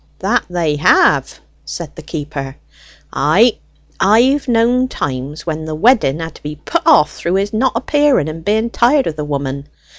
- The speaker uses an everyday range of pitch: No, wide, 8.2 semitones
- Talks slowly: No, average, 160 wpm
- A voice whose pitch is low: No, medium, 170 Hz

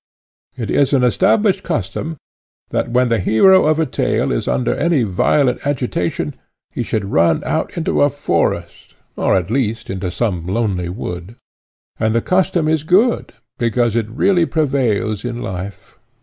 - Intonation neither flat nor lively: No, wide, 7.3 semitones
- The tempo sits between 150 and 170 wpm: Yes, average, 155 wpm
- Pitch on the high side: No, low, 115 Hz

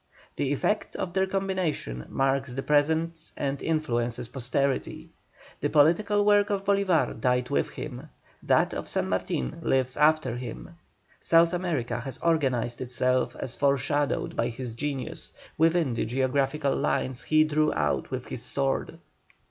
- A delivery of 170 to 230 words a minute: No, average, 140 wpm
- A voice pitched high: No, medium, 140 Hz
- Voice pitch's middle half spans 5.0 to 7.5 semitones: No, average, 4.5 semitones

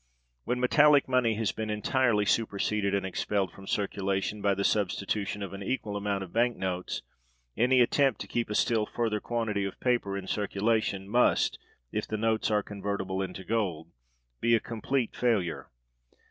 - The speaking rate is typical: Yes, average, 165 wpm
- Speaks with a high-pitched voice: No, low, 105 Hz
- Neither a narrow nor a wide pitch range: Yes, average, 3.0 semitones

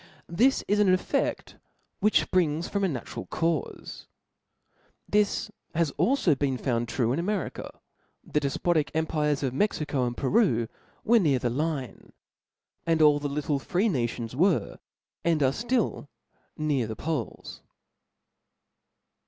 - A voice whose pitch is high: No, medium, 155 Hz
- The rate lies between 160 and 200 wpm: No, slow, 135 wpm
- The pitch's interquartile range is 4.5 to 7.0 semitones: Yes, wide, 5.4 semitones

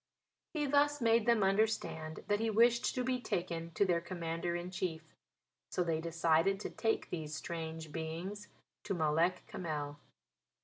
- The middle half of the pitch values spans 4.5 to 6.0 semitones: Yes, average, 5.2 semitones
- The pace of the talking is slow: No, average, 150 wpm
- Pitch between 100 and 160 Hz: No, medium, 175 Hz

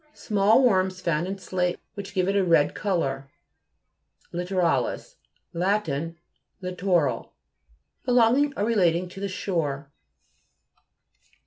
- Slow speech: Yes, slow, 115 wpm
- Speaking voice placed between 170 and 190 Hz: Yes, medium, 185 Hz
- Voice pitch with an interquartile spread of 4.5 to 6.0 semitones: No, average, 2.9 semitones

